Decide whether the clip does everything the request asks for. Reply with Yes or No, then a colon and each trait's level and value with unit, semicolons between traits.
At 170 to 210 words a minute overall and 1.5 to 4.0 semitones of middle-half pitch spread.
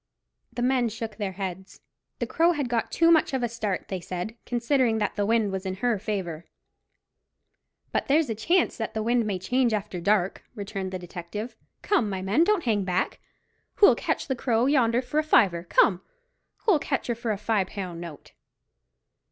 No: average, 190 wpm; average, 4.4 semitones